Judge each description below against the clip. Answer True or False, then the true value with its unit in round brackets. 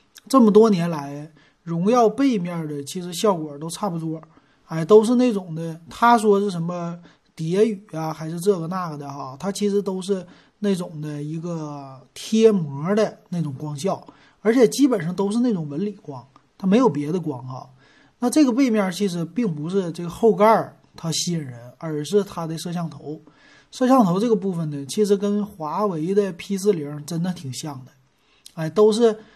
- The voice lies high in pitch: False (175 Hz)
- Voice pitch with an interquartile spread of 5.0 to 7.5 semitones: True (5.3 semitones)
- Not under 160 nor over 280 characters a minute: True (260 characters per minute)